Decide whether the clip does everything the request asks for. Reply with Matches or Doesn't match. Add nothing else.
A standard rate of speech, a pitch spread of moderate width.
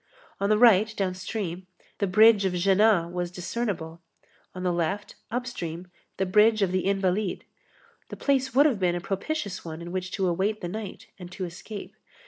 Matches